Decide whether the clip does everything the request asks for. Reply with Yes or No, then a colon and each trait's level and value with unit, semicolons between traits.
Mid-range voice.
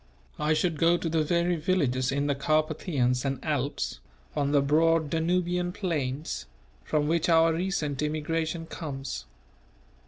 Yes: medium, 155 Hz